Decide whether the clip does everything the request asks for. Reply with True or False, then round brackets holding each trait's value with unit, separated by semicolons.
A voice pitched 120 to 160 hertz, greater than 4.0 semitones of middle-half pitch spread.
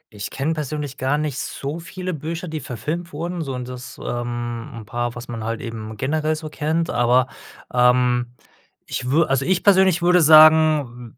True (140 Hz; 4.7 semitones)